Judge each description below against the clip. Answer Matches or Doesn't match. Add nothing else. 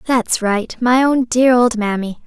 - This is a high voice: Matches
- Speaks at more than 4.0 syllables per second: Doesn't match